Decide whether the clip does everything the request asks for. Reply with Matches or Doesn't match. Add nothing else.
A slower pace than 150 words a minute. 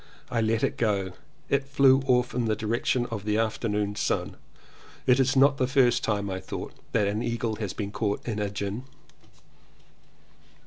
Doesn't match